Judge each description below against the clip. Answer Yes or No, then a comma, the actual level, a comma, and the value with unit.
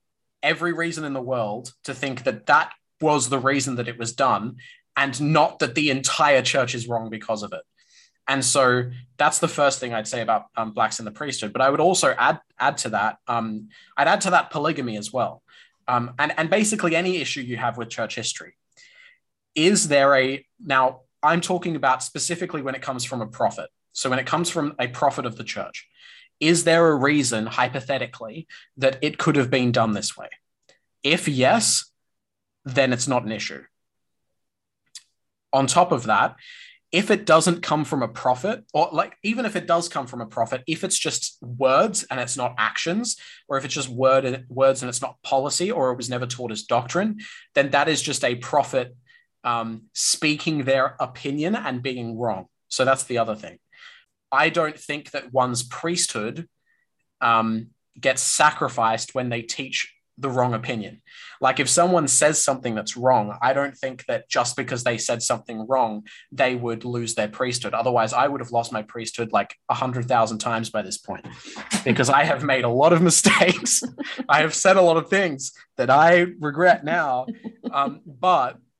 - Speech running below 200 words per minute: Yes, average, 190 wpm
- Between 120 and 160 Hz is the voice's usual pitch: Yes, low, 135 Hz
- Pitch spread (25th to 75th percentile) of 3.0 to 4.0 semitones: No, average, 4.6 semitones